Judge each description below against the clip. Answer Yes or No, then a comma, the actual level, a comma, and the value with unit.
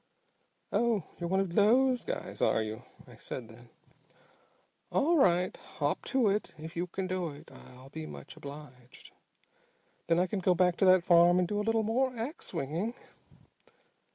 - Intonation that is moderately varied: No, wide, 6.5 semitones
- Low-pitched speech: No, medium, 180 Hz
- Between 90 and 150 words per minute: No, average, 170 wpm